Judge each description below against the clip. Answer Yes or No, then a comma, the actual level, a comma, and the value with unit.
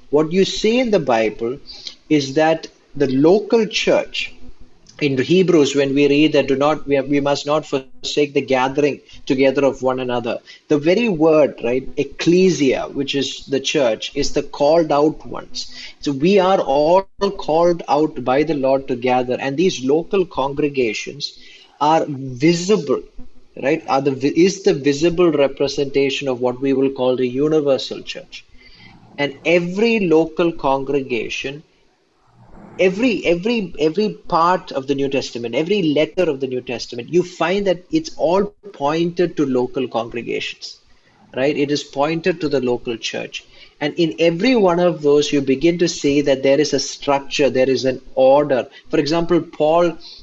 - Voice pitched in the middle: Yes, medium, 145 Hz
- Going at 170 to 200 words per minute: No, average, 160 wpm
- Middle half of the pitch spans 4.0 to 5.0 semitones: Yes, average, 4.3 semitones